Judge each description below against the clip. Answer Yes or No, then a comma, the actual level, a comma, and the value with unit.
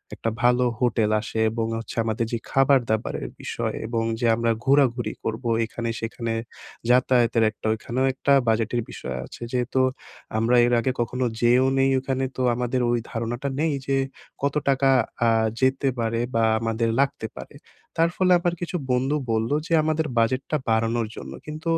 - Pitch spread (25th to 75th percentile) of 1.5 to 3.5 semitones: Yes, average, 2.8 semitones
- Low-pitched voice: Yes, low, 120 Hz